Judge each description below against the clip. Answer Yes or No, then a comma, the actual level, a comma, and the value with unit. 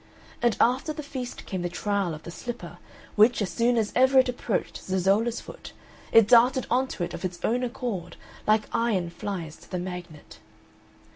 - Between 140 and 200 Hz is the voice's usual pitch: No, high, 215 Hz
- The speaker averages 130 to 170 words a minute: No, average, 185 wpm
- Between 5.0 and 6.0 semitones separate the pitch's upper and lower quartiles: Yes, average, 5.3 semitones